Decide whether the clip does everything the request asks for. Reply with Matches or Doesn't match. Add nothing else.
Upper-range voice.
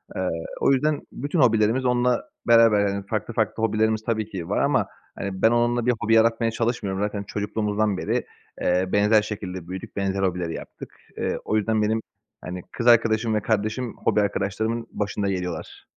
Doesn't match